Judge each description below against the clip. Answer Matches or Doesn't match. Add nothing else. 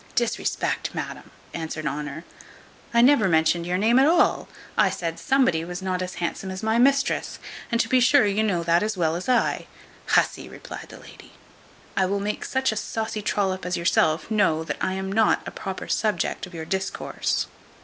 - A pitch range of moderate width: Matches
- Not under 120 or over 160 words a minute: Doesn't match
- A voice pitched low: Doesn't match